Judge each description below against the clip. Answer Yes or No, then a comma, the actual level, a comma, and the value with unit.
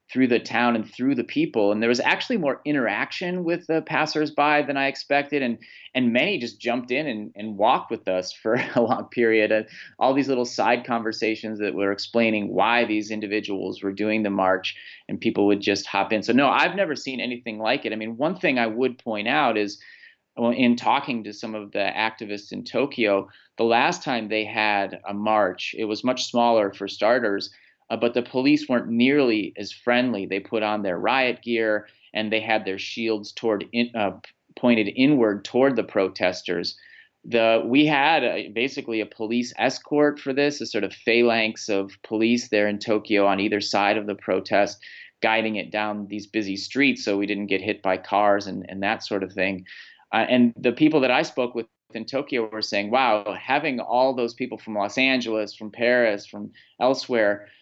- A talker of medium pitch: No, low, 110 Hz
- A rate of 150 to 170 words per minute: No, average, 200 wpm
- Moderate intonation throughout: Yes, average, 3.1 semitones